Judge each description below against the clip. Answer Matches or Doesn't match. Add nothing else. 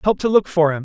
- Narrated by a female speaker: Doesn't match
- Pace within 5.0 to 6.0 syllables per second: Doesn't match